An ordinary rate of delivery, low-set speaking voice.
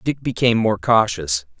Yes: average, 150 wpm; low, 105 Hz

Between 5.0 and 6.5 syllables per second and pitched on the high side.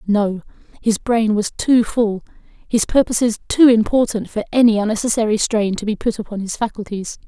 Yes: 5.3 syllables/s; high, 220 Hz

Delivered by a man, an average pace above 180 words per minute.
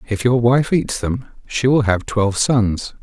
Yes: male; average, 200 wpm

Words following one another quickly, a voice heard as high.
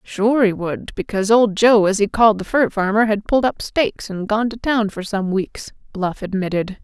Yes: fast, 220 wpm; high, 210 Hz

